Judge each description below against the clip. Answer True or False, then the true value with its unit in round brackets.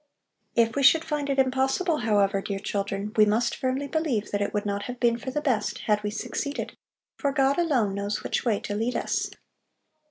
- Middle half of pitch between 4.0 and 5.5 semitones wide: True (5.1 semitones)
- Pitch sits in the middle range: False (235 Hz)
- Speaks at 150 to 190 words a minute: False (200 wpm)